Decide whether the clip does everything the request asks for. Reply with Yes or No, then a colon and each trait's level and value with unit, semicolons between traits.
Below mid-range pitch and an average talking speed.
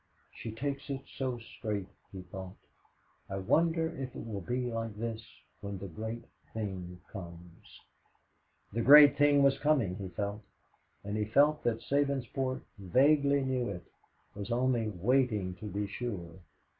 Yes: low, 115 Hz; average, 145 wpm